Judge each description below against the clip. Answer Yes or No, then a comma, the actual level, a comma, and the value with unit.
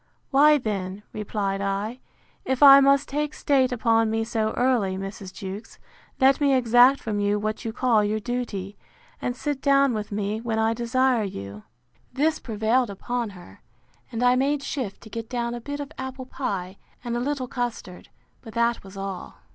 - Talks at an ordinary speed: Yes, average, 180 wpm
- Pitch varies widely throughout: No, average, 4.1 semitones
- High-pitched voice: Yes, high, 230 Hz